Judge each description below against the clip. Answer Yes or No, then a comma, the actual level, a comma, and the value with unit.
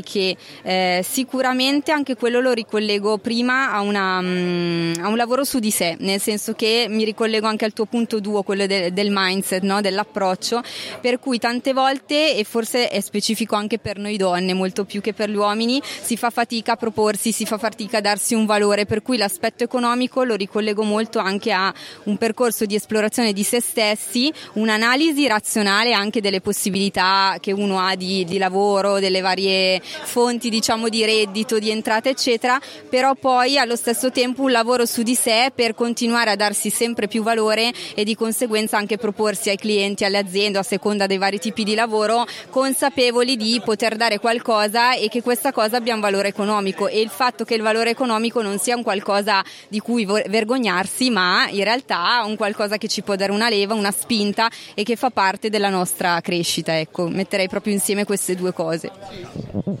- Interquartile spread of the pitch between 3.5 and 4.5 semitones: No, average, 2.9 semitones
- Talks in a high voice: Yes, high, 220 Hz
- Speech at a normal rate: No, fast, 185 wpm